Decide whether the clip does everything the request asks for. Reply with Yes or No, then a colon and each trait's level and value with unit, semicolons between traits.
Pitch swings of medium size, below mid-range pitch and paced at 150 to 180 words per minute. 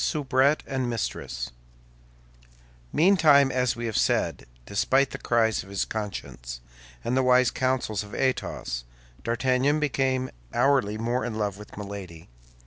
No: average, 4.1 semitones; low, 125 Hz; slow, 135 wpm